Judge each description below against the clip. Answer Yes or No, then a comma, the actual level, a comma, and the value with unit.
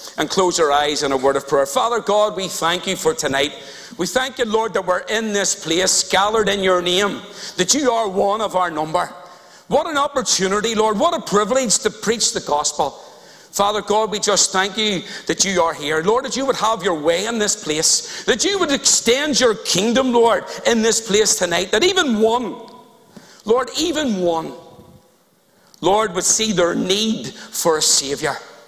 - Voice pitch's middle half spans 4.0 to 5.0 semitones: Yes, average, 4.5 semitones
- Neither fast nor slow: Yes, average, 190 wpm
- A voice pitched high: Yes, high, 205 Hz